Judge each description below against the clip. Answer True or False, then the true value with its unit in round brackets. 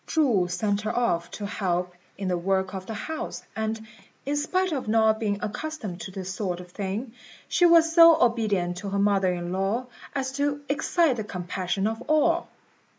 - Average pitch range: False (6.6 semitones)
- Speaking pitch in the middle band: False (210 Hz)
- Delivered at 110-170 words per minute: False (185 wpm)